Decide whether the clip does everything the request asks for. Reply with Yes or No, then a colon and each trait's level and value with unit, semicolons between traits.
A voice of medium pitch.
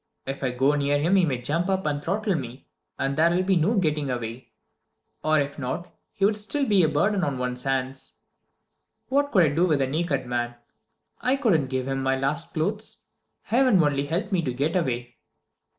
Yes: medium, 150 Hz